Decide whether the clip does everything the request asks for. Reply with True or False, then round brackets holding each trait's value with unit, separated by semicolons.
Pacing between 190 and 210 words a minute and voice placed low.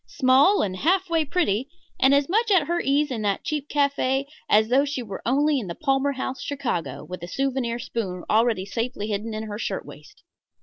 False (205 wpm; 260 Hz)